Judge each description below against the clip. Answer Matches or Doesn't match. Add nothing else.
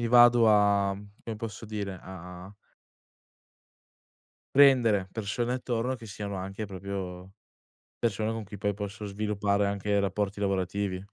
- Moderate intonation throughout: Doesn't match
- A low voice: Matches